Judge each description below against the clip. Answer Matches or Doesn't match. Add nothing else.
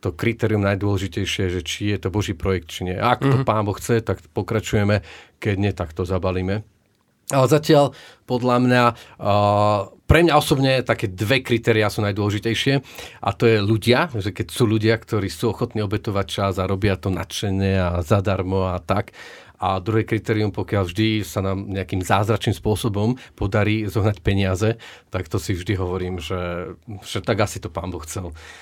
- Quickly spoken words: Matches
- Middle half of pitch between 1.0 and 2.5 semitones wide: Doesn't match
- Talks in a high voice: Doesn't match